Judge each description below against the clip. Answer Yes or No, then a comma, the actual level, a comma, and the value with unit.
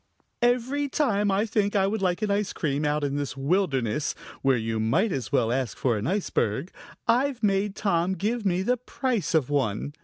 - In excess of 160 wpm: Yes, average, 190 wpm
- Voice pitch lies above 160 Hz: Yes, high, 190 Hz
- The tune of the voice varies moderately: No, wide, 7.4 semitones